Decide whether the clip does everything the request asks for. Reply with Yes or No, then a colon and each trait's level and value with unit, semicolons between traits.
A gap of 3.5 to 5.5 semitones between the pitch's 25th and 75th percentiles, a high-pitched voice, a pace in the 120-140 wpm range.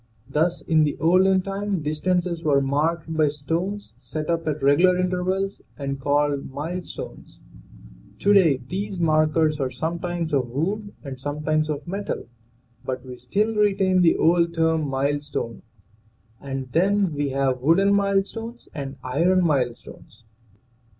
No: average, 4.4 semitones; medium, 160 Hz; slow, 135 wpm